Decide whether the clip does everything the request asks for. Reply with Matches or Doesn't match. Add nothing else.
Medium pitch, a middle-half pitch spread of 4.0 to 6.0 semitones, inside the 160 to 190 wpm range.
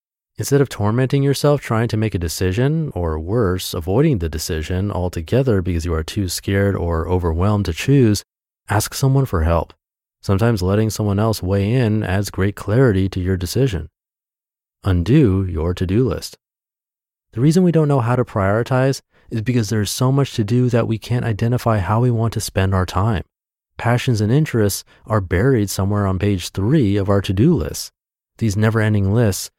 Doesn't match